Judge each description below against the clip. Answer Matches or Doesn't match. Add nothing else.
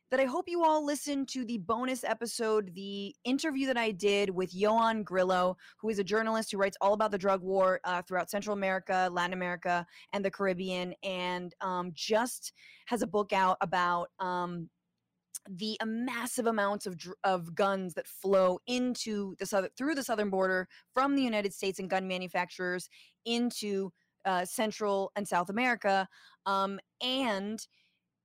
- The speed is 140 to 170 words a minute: Matches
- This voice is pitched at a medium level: Doesn't match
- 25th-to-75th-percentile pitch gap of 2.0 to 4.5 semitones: Matches